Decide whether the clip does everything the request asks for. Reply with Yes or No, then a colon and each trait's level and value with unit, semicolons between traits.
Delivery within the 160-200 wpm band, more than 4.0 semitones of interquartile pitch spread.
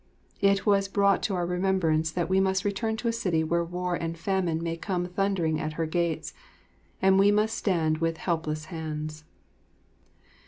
No: average, 170 wpm; average, 3.2 semitones